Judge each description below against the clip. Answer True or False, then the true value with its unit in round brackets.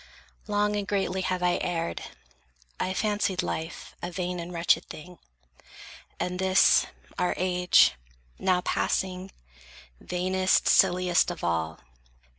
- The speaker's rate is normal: False (115 wpm)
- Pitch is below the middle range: False (180 Hz)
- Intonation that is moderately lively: False (1.1 semitones)